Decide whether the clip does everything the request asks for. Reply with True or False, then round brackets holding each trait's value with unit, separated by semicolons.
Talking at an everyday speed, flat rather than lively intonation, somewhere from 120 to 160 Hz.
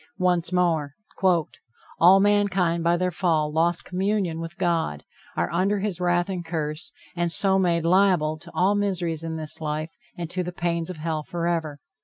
False (170 wpm; 2.1 semitones; 170 Hz)